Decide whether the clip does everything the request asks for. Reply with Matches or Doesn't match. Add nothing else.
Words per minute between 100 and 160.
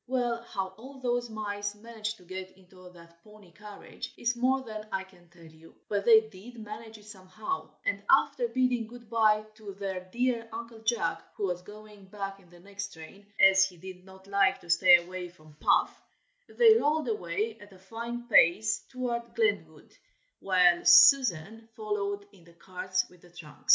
Doesn't match